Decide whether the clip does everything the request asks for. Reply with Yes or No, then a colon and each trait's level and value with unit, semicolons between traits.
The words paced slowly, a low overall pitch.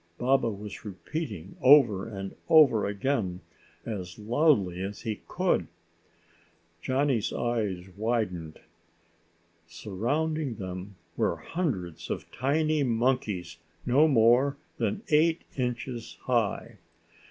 Yes: slow, 95 wpm; low, 115 Hz